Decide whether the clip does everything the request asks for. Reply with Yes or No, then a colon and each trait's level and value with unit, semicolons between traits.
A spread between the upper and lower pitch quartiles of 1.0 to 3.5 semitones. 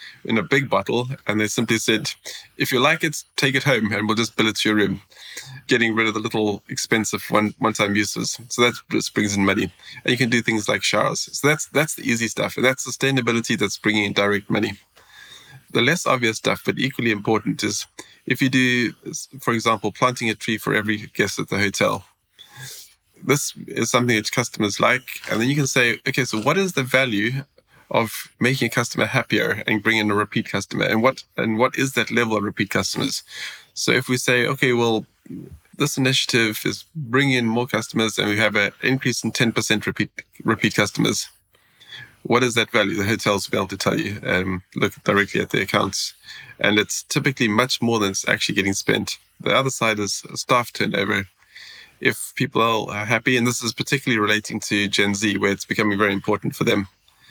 Yes: average, 3.1 semitones